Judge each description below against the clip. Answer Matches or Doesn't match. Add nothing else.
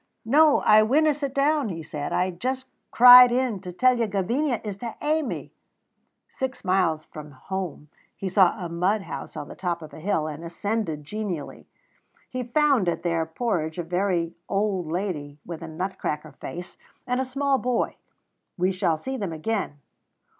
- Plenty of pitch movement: Matches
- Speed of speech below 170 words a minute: Doesn't match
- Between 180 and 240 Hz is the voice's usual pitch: Matches